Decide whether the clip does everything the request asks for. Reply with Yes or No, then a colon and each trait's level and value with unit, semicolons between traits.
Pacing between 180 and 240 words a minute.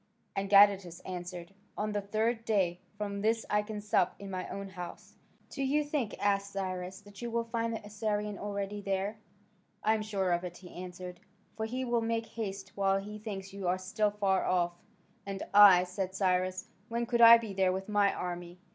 Yes: average, 195 wpm